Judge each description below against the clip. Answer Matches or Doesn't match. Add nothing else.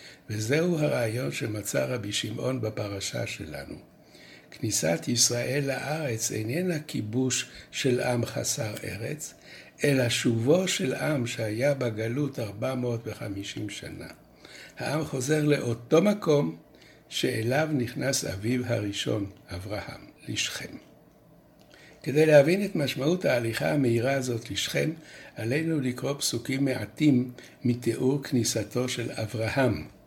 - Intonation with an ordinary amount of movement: Matches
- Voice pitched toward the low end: Matches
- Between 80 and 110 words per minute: Matches